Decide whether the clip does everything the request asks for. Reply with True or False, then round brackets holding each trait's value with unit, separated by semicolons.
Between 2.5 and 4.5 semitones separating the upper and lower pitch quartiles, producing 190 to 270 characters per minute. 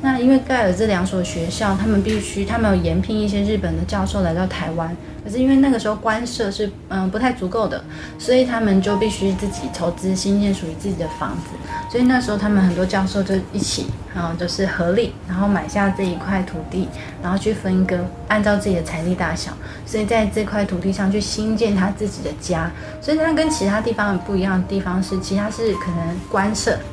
False (3.0 semitones; 335 characters per minute)